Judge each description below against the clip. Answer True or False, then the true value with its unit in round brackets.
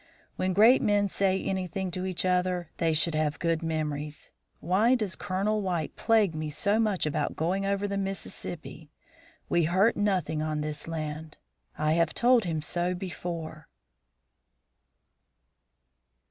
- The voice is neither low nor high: True (180 Hz)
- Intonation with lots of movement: False (3.8 semitones)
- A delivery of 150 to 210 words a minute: False (140 wpm)